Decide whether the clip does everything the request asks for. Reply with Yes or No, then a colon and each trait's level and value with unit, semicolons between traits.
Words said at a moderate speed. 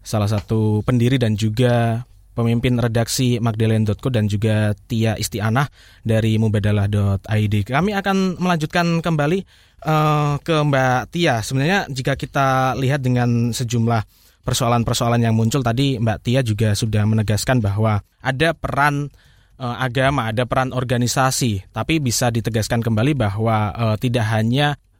Yes: average, 125 wpm